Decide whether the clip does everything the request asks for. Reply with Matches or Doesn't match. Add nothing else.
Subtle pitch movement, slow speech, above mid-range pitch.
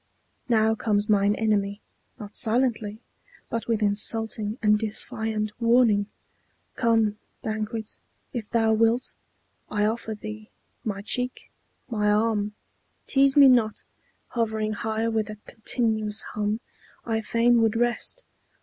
Matches